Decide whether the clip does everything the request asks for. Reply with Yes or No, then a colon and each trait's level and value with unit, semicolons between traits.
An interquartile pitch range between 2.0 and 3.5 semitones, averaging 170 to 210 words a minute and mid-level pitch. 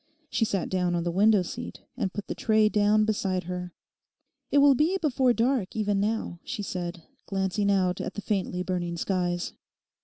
No: average, 3.2 semitones; average, 180 wpm; high, 195 Hz